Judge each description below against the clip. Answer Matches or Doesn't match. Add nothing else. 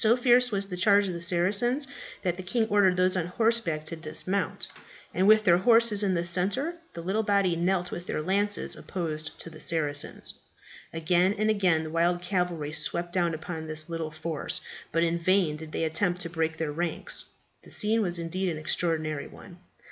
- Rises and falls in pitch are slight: Doesn't match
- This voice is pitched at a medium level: Matches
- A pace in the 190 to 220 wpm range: Matches